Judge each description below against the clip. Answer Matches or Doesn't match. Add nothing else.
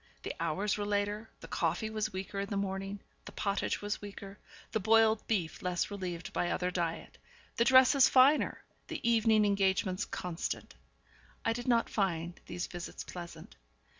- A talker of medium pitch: Doesn't match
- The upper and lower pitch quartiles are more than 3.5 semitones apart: Doesn't match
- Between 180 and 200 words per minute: Doesn't match